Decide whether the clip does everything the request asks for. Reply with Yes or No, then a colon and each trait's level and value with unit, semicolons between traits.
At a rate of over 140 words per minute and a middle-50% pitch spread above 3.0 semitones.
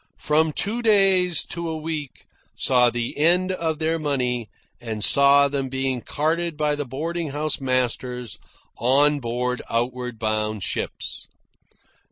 No: slow, 135 wpm; average, 4.4 semitones